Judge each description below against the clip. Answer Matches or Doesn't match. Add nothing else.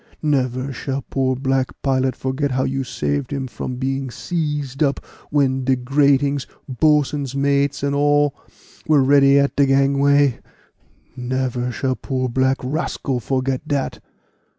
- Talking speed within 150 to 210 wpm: Doesn't match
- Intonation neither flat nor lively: Doesn't match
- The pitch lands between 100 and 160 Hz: Matches